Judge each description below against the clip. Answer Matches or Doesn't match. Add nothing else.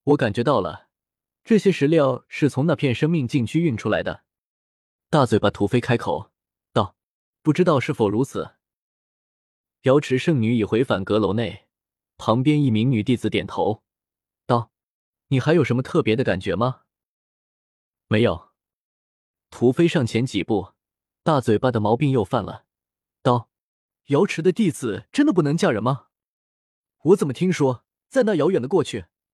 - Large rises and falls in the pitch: Matches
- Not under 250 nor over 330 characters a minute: Doesn't match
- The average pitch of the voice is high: Doesn't match